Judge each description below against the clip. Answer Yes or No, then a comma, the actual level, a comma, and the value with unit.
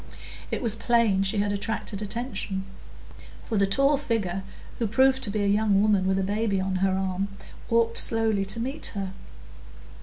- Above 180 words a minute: No, average, 175 wpm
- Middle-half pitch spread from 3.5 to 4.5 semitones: No, average, 2.9 semitones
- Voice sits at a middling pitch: No, high, 205 Hz